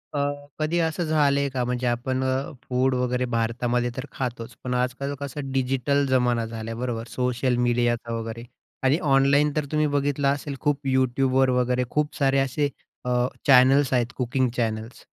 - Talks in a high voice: No, low, 130 Hz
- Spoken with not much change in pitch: Yes, narrow, 2.3 semitones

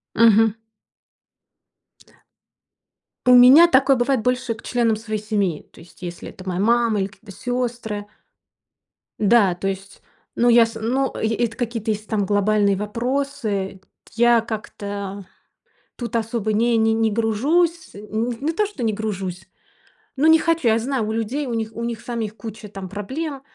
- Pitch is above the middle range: Yes, high, 225 Hz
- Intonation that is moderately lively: Yes, average, 3.0 semitones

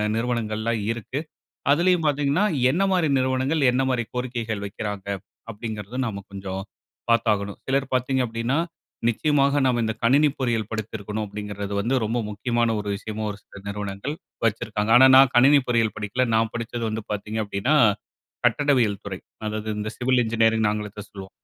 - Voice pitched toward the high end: No, low, 115 Hz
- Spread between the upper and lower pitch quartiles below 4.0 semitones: Yes, average, 3.5 semitones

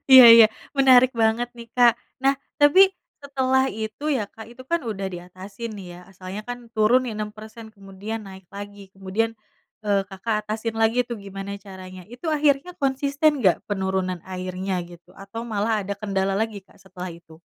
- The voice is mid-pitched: No, high, 215 Hz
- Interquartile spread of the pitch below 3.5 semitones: No, average, 4.0 semitones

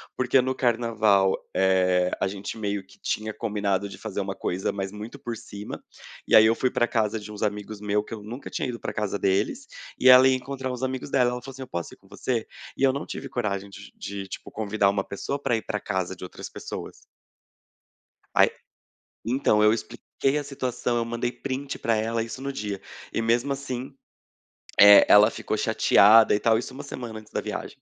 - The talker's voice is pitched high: No, low, 110 Hz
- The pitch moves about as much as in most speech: Yes, average, 3.8 semitones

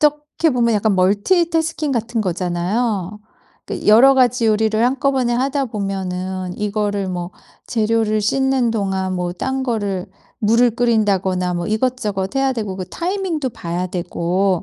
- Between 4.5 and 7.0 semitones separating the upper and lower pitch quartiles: Yes, average, 5.1 semitones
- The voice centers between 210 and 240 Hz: Yes, high, 215 Hz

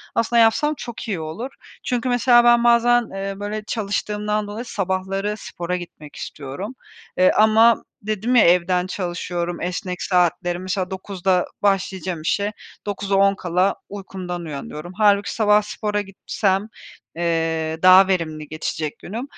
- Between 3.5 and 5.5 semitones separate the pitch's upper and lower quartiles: No, average, 3.1 semitones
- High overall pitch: Yes, high, 195 Hz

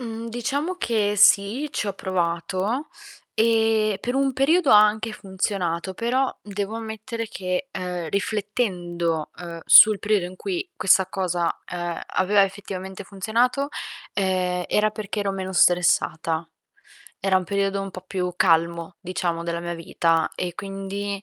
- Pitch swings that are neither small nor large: Yes, average, 3.5 semitones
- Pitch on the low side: No, high, 195 Hz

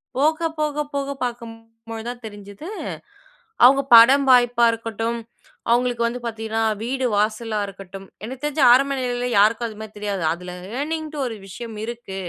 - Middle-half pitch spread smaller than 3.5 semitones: Yes, average, 3.0 semitones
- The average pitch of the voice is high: Yes, high, 235 Hz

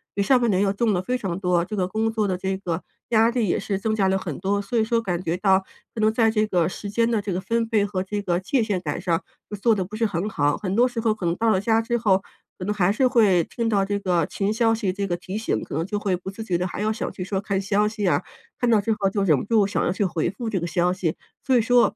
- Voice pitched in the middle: No, high, 200 Hz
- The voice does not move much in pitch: No, average, 3.1 semitones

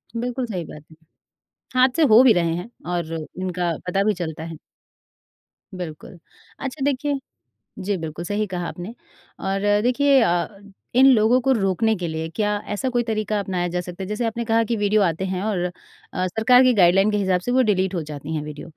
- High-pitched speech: Yes, high, 195 Hz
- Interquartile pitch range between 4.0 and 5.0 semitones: Yes, average, 4.6 semitones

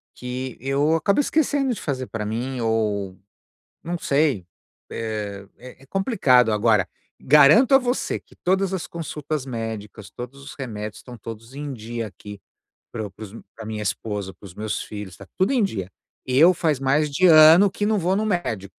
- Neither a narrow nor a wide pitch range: No, wide, 7.4 semitones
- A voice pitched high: No, low, 130 Hz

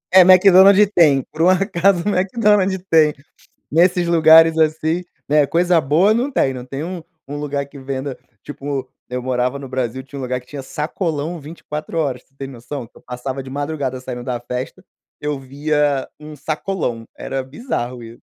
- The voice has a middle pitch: Yes, medium, 145 Hz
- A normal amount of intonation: Yes, average, 4.6 semitones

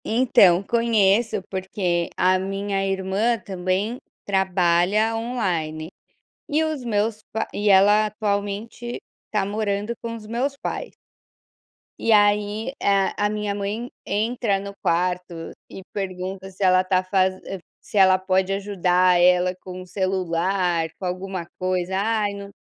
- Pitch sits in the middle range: No, high, 195 Hz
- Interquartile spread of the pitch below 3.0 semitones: Yes, narrow, 2.5 semitones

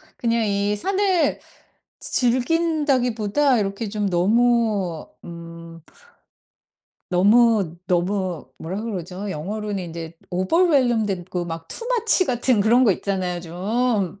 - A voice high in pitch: Yes, high, 205 Hz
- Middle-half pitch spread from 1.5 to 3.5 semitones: No, average, 5.3 semitones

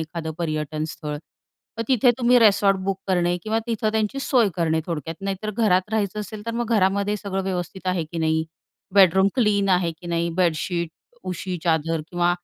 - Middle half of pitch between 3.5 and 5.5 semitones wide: Yes, average, 3.8 semitones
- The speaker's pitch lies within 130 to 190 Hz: Yes, medium, 185 Hz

